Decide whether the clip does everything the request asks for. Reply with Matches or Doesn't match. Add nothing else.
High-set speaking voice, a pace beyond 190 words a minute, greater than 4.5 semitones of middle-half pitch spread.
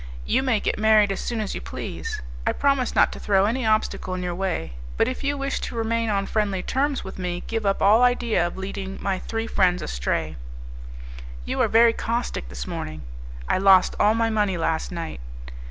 Doesn't match